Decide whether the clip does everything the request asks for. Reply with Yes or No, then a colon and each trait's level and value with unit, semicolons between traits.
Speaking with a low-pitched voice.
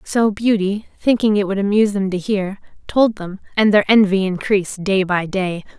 No: high, 200 Hz